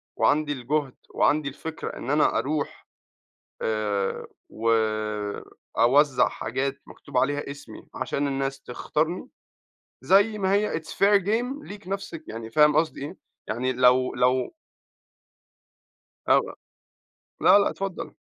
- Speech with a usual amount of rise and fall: No, wide, 5.7 semitones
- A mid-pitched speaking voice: Yes, medium, 145 Hz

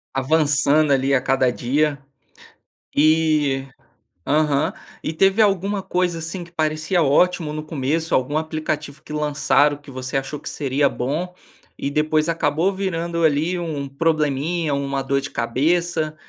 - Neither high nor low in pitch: Yes, medium, 155 Hz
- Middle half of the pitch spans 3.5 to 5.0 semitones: No, average, 2.9 semitones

